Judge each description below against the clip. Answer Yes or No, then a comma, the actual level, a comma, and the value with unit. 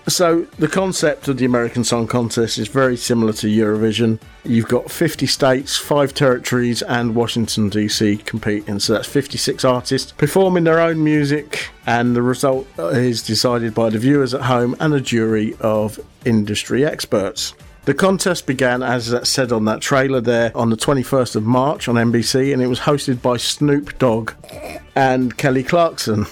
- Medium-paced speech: Yes, average, 170 wpm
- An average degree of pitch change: Yes, average, 3.3 semitones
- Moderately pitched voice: No, low, 125 Hz